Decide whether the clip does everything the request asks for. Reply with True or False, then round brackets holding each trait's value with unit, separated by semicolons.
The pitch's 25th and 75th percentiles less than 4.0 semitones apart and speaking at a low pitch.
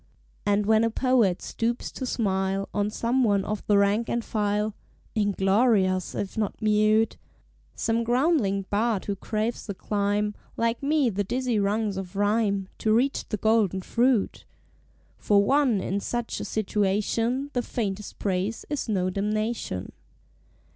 False (2.6 semitones; 215 Hz)